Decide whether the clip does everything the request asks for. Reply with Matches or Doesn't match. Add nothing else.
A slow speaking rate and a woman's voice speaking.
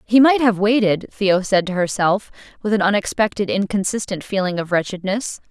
Doesn't match